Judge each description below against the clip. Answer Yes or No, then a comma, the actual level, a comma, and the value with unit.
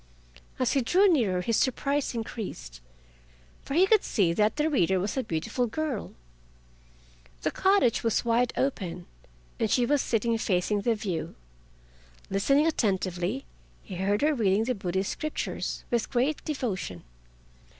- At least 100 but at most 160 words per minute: Yes, average, 140 wpm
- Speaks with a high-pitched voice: Yes, high, 230 Hz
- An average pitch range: No, wide, 6.3 semitones